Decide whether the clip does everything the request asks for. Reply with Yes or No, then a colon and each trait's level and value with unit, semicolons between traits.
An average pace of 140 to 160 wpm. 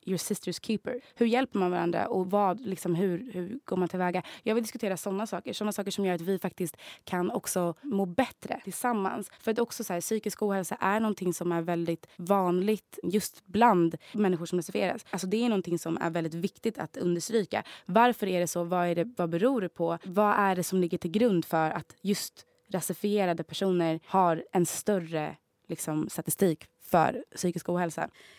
No: average, 190 wpm